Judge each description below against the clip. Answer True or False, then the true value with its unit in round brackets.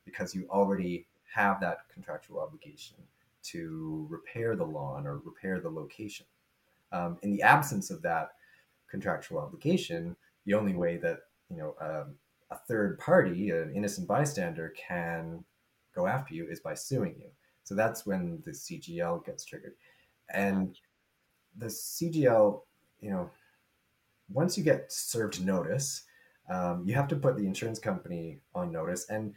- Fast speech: False (145 wpm)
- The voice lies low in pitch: True (105 Hz)